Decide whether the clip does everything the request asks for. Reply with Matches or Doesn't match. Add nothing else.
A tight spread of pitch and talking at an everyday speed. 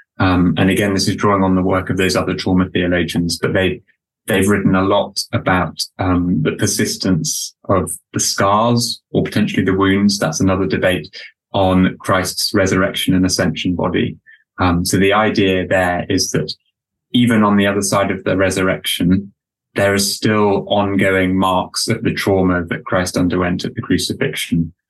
Matches